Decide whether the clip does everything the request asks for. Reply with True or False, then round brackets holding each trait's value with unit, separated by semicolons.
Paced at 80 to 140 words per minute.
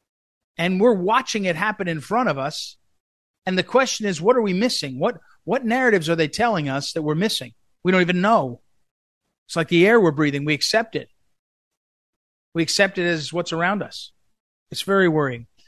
False (190 wpm)